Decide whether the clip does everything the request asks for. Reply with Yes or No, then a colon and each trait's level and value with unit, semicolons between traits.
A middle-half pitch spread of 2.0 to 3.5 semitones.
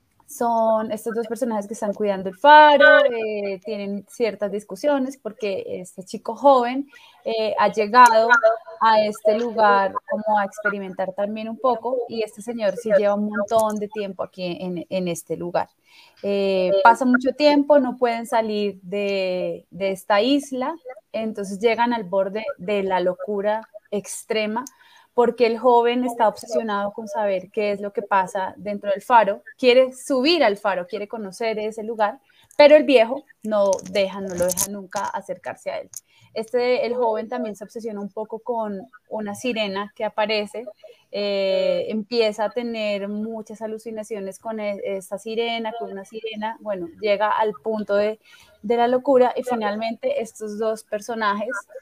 Yes: average, 2.9 semitones